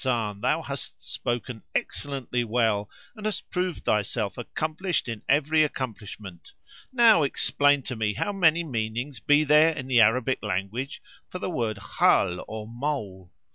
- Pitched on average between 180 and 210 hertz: No, low, 125 Hz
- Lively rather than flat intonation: Yes, wide, 5.7 semitones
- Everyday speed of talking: Yes, average, 150 wpm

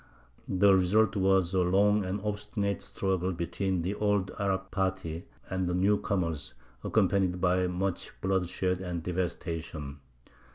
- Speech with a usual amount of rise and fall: No, narrow, 1.8 semitones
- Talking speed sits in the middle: No, slow, 130 wpm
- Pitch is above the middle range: No, very low, 95 Hz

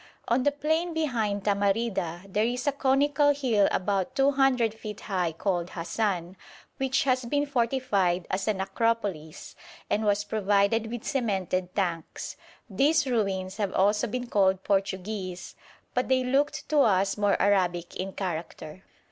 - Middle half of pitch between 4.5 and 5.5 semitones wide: Yes, average, 5.2 semitones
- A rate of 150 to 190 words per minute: No, average, 140 wpm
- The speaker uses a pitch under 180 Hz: No, high, 210 Hz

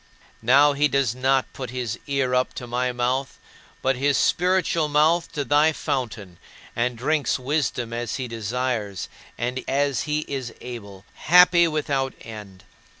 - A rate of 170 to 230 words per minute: No, average, 150 wpm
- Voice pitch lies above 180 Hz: No, low, 130 Hz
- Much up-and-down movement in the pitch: No, average, 3.3 semitones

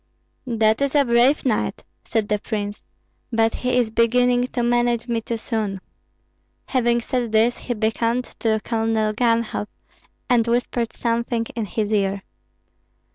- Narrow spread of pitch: Yes, narrow, 1.7 semitones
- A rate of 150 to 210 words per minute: No, average, 140 wpm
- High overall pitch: Yes, high, 230 Hz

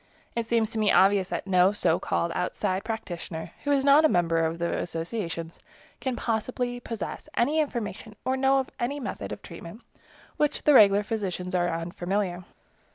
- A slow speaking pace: No, average, 175 wpm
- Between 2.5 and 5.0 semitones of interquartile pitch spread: No, wide, 5.6 semitones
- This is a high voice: Yes, high, 205 Hz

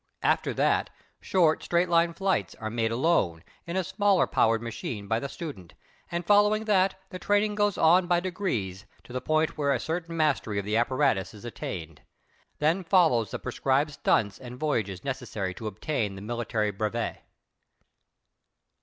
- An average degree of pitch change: No, wide, 8.0 semitones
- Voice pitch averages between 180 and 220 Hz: No, low, 135 Hz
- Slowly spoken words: No, average, 165 wpm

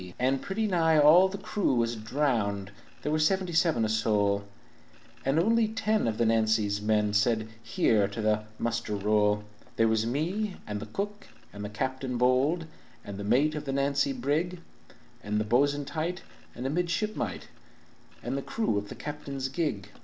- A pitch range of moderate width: No, wide, 6.8 semitones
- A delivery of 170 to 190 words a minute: Yes, average, 175 wpm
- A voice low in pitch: Yes, low, 130 Hz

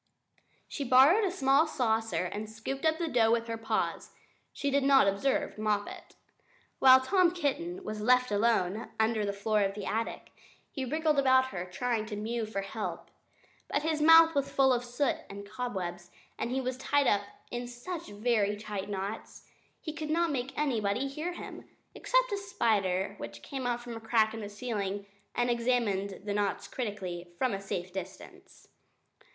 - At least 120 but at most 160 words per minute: No, average, 175 wpm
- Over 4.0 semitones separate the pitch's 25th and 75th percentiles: Yes, average, 5.1 semitones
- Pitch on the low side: No, high, 235 Hz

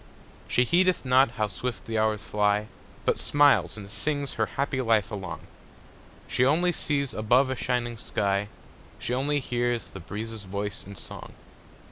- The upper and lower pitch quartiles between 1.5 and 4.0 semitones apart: No, average, 4.4 semitones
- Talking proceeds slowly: No, average, 155 wpm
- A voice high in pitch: No, low, 115 Hz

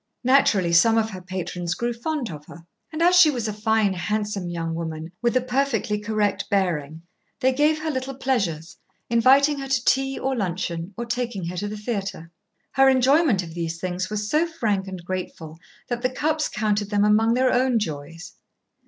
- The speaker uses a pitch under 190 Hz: No, high, 210 Hz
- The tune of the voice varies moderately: No, wide, 6.3 semitones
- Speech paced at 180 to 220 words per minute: Yes, average, 190 wpm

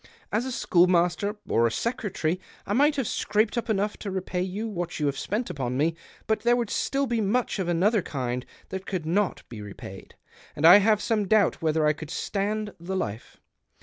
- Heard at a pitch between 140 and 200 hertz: Yes, high, 190 Hz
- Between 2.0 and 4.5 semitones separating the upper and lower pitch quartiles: No, average, 5.1 semitones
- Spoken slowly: No, average, 200 wpm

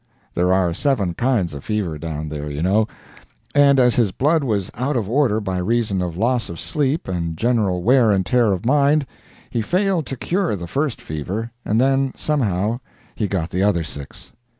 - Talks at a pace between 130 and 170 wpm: No, average, 190 wpm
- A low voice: Yes, low, 110 Hz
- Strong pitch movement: Yes, wide, 6.7 semitones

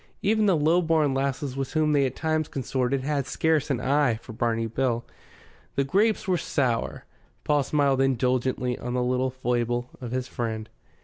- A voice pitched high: No, low, 135 Hz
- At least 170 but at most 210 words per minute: Yes, average, 175 wpm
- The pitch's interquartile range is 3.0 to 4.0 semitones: Yes, average, 3.3 semitones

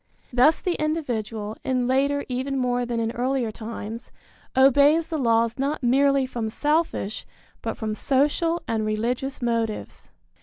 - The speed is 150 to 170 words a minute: No, average, 140 wpm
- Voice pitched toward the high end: Yes, very high, 255 Hz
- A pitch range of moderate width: Yes, average, 3.6 semitones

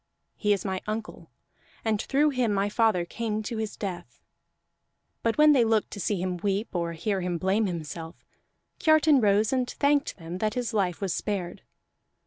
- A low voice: No, high, 210 Hz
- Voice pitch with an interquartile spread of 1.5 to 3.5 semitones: No, average, 4.0 semitones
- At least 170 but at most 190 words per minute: Yes, average, 175 wpm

